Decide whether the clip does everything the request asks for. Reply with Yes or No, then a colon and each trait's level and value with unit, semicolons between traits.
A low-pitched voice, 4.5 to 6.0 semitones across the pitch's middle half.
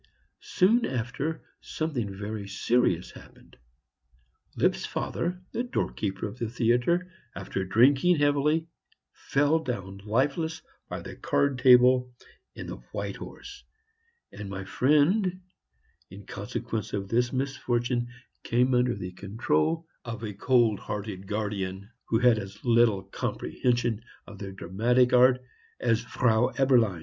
Yes: low, 120 Hz; average, 4.8 semitones